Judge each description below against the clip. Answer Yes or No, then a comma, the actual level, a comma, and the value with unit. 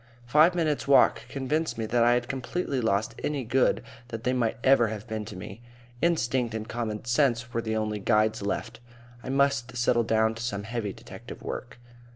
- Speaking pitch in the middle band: No, low, 120 Hz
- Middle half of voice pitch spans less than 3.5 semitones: Yes, average, 3.1 semitones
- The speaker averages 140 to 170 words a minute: No, average, 190 wpm